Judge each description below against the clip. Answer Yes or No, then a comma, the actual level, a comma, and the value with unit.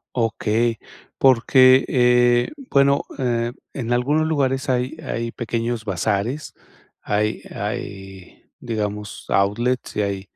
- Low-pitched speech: Yes, low, 120 Hz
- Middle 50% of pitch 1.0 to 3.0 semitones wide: No, average, 3.4 semitones